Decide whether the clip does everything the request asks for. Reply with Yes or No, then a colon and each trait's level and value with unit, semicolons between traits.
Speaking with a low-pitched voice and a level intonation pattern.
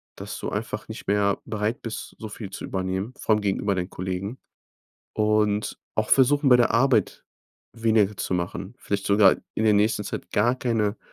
Yes: low, 105 Hz; narrow, 2.3 semitones